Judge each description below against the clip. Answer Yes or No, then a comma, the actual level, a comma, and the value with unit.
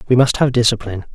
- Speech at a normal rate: No, fast, 210 wpm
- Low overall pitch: Yes, low, 120 Hz